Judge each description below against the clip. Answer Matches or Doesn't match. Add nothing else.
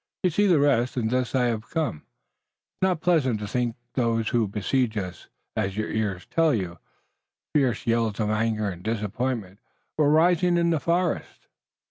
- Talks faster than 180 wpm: Doesn't match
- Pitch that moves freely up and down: Matches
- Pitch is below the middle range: Matches